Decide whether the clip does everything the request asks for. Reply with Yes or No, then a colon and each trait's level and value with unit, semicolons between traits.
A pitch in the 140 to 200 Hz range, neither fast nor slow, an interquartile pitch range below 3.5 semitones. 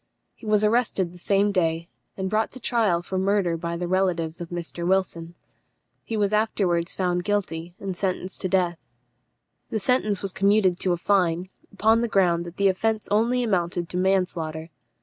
Yes: medium, 185 Hz; average, 175 wpm; average, 3.0 semitones